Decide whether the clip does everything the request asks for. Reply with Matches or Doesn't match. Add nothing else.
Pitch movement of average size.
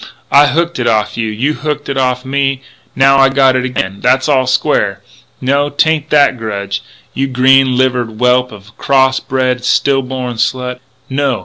Doesn't match